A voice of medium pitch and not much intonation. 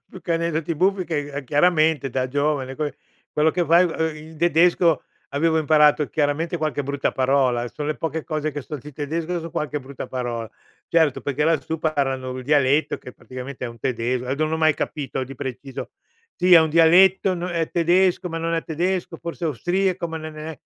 No: medium, 155 Hz; average, 3.2 semitones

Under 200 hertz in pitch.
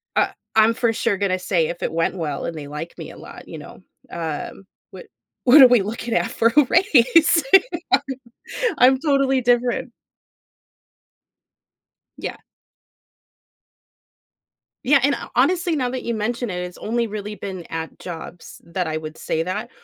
No: high, 225 Hz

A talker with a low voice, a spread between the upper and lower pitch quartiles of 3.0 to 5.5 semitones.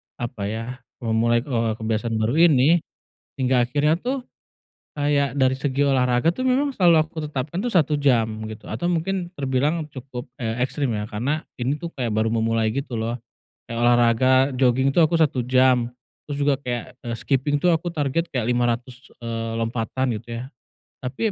Yes: low, 130 Hz; average, 4.1 semitones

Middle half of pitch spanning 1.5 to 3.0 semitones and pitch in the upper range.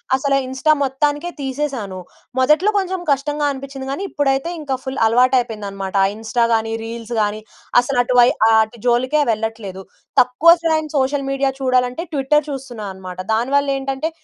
No: average, 3.6 semitones; very high, 265 Hz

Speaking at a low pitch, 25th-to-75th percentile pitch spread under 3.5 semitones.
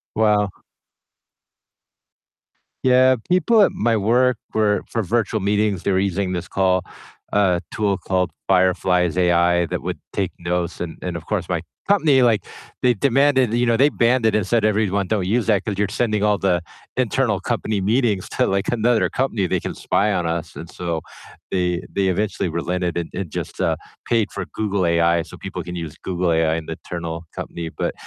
No: low, 100 Hz; average, 4.0 semitones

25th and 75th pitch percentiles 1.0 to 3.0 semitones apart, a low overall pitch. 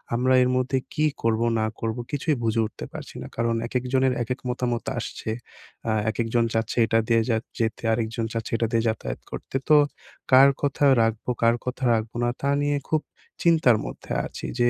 Yes: narrow, 2.4 semitones; low, 120 Hz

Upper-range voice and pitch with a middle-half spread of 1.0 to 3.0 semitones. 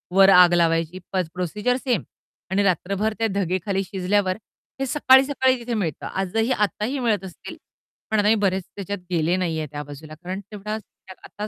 No: high, 195 Hz; average, 3.4 semitones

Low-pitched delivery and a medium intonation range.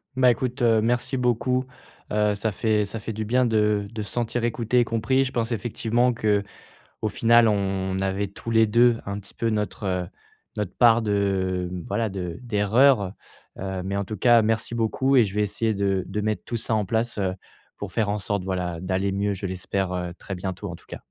Yes: low, 105 Hz; average, 3.0 semitones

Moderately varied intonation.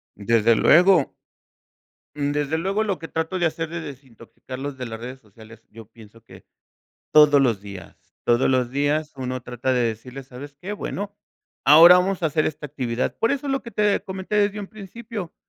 No: wide, 6.9 semitones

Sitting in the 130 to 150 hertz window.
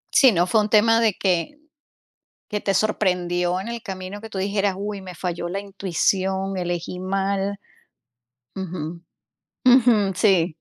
No: high, 195 Hz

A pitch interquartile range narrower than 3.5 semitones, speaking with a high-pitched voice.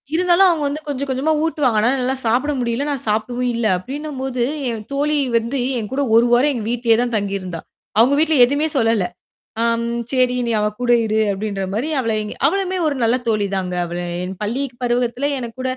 No: average, 4.0 semitones; high, 245 Hz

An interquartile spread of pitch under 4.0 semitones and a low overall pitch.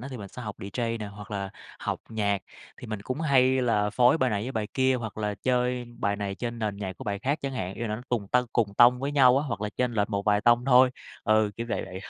Yes: average, 3.5 semitones; low, 115 Hz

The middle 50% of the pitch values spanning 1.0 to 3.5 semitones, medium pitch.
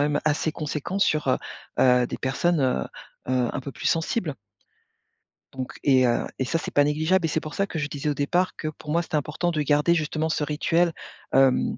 Yes: average, 3.1 semitones; medium, 150 Hz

